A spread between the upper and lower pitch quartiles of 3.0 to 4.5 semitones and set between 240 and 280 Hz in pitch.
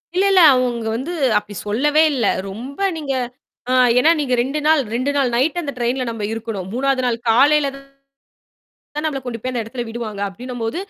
Yes: average, 3.7 semitones; very high, 250 Hz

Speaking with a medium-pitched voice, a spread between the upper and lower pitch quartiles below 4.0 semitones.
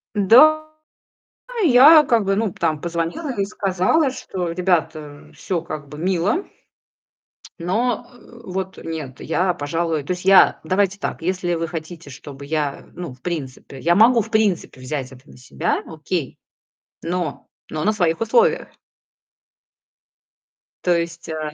No: medium, 175 Hz; average, 4.3 semitones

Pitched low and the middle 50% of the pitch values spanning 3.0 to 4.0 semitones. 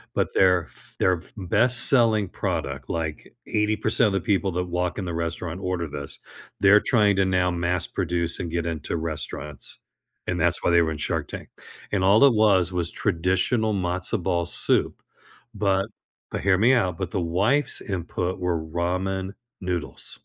No: very low, 90 Hz; narrow, 2.6 semitones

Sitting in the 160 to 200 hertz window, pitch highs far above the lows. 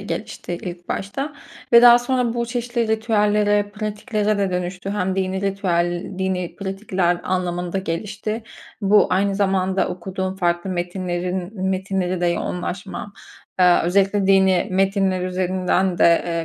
No: high, 190 Hz; narrow, 2.4 semitones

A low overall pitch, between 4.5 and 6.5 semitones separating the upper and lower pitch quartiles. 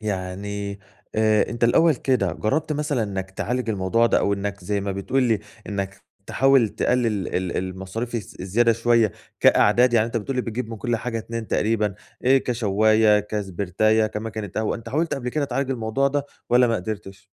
No: low, 110 Hz; average, 3.2 semitones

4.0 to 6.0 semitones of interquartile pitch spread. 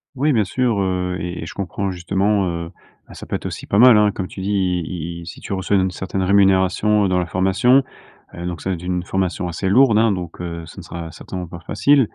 No: narrow, 2.5 semitones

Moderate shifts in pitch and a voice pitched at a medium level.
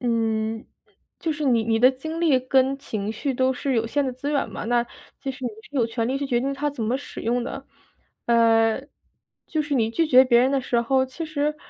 No: average, 3.3 semitones; very high, 255 Hz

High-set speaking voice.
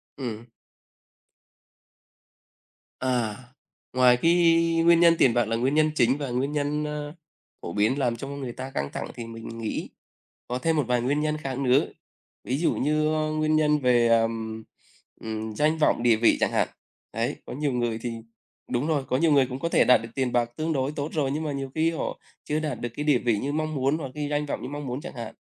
No: low, 135 Hz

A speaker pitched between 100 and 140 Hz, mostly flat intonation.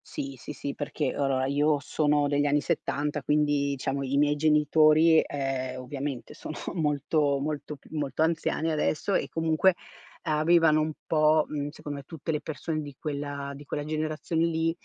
No: medium, 150 Hz; narrow, 1.7 semitones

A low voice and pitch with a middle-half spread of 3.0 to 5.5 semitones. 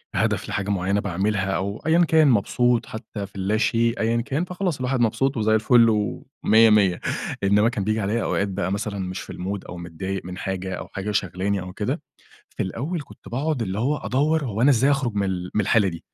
Yes: low, 105 Hz; average, 4.1 semitones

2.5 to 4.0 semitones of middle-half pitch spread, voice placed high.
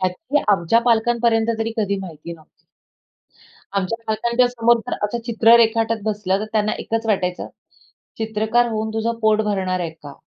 Yes: average, 2.9 semitones; high, 220 Hz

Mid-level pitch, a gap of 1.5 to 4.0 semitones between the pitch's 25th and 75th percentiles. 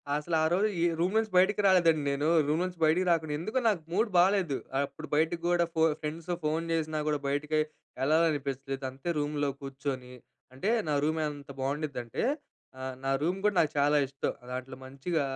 Yes: medium, 155 Hz; average, 3.6 semitones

